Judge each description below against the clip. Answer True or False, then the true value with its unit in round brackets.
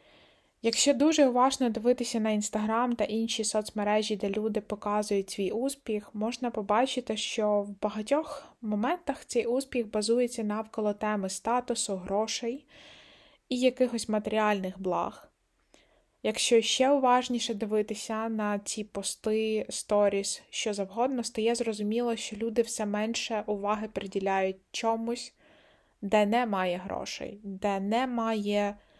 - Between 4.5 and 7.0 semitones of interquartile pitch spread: False (2.4 semitones)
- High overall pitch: True (220 Hz)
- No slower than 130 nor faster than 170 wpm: False (115 wpm)